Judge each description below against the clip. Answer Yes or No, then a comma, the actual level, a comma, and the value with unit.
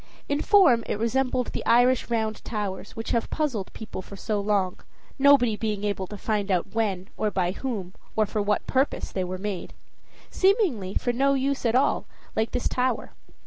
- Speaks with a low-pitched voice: No, high, 220 Hz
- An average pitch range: Yes, average, 4.1 semitones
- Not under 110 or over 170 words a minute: No, average, 185 wpm